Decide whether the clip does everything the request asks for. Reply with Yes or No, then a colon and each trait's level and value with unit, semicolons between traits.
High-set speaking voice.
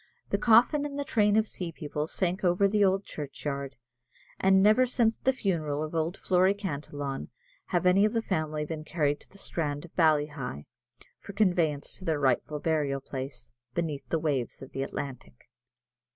No: medium, 160 Hz